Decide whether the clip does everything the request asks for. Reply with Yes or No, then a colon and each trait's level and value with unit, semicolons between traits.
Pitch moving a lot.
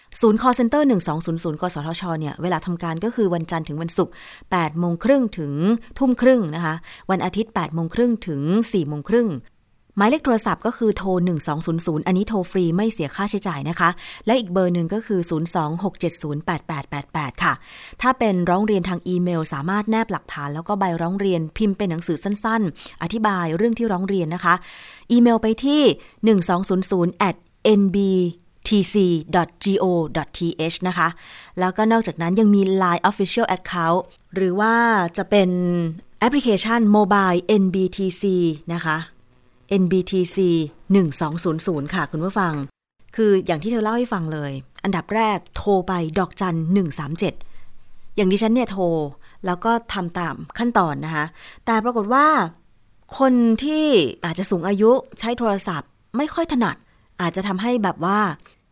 No: average, 4.2 semitones